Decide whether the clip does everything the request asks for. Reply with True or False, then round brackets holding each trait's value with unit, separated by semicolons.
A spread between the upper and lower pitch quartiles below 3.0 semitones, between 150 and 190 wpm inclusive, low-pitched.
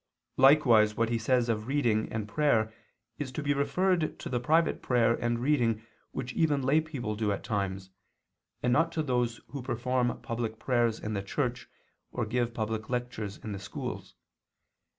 False (3.7 semitones; 170 wpm; 120 Hz)